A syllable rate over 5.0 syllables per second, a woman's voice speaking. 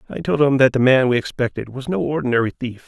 No: 6.5 syllables/s; male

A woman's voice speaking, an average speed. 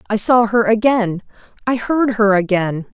Yes: female; average, 160 wpm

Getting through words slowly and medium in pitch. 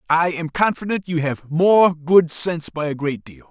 No: fast, 205 wpm; medium, 160 Hz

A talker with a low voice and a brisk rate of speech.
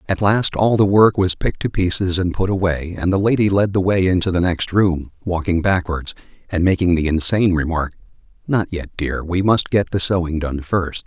Yes: very low, 90 Hz; fast, 210 wpm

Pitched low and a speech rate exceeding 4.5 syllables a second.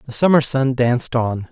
Yes: low, 130 Hz; 5.1 syllables/s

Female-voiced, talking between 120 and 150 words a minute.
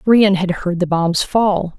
No: female; average, 200 wpm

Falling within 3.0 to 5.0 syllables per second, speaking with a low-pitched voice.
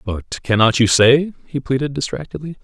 No: 5.3 syllables/s; low, 130 Hz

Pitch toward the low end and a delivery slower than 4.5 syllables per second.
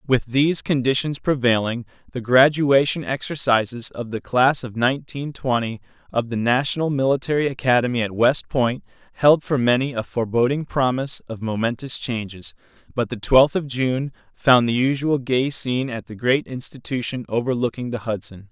No: low, 125 Hz; 5.1 syllables/s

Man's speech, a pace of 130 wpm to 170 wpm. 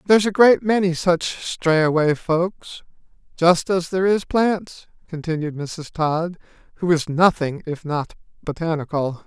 Yes: male; slow, 135 wpm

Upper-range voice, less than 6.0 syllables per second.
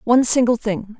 Yes: high, 230 Hz; 5.6 syllables/s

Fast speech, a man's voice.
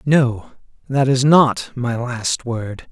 No: average, 145 wpm; male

